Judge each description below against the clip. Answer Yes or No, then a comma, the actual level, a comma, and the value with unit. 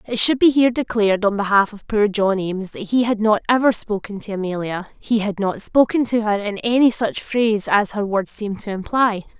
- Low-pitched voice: No, high, 210 Hz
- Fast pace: Yes, fast, 215 wpm